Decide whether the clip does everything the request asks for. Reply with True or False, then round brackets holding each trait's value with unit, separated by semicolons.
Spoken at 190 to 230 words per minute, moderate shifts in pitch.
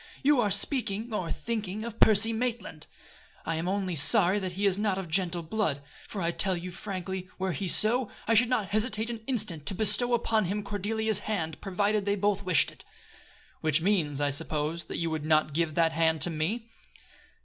True (195 wpm; 4.5 semitones)